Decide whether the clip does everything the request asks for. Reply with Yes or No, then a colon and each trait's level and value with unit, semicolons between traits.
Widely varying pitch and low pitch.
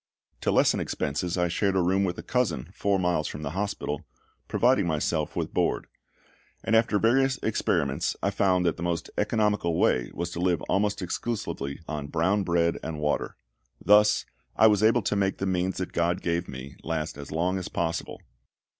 No: average, 3.7 semitones; very low, 90 Hz